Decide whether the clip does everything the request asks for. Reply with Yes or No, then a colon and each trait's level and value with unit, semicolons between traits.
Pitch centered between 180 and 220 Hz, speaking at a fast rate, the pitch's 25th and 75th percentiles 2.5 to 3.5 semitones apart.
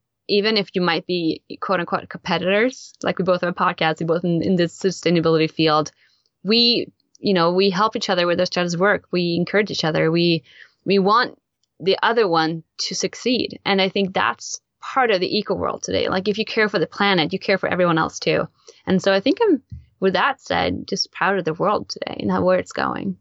Yes: medium, 185 Hz; fast, 220 wpm; average, 3.0 semitones